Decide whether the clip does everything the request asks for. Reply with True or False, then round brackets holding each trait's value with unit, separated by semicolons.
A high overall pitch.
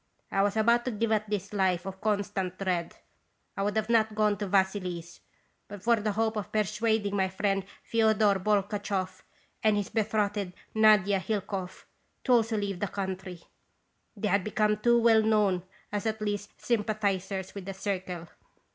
True (205 Hz)